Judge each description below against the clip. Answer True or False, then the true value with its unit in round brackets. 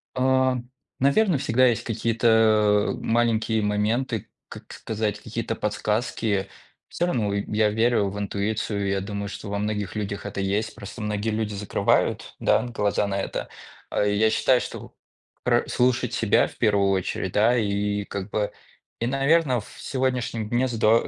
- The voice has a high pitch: False (110 Hz)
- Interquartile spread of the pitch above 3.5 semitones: False (2.7 semitones)